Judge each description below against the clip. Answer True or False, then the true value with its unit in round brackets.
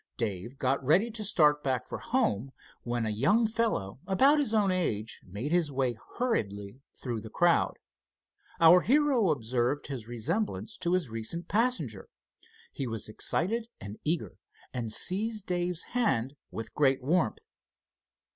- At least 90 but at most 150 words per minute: True (145 wpm)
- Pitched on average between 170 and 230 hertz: False (150 Hz)